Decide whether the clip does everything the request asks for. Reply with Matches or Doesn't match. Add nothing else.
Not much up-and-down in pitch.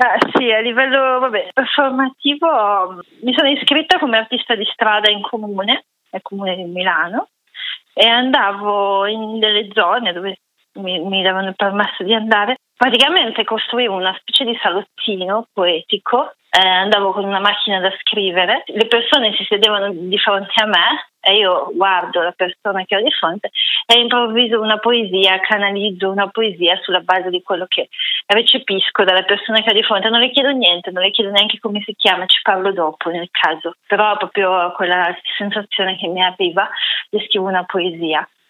Doesn't match